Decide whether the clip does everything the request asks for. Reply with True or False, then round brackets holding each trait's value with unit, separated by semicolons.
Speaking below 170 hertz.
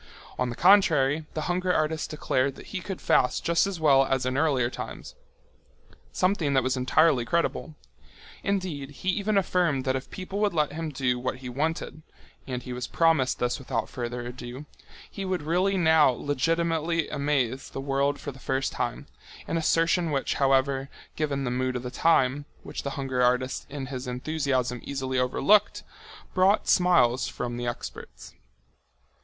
True (140 Hz)